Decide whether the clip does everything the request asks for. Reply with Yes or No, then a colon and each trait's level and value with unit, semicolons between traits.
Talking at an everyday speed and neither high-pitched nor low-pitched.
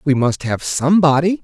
Yes: average, 170 wpm; medium, 155 Hz